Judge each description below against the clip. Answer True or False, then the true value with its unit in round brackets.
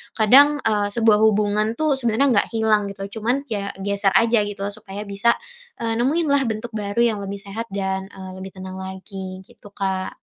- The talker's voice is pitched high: True (210 Hz)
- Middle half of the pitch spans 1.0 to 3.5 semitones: True (2.7 semitones)